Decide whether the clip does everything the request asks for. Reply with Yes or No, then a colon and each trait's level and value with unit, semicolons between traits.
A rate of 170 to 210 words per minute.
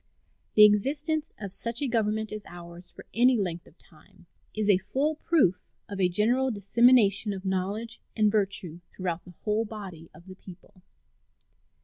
No: average, 160 wpm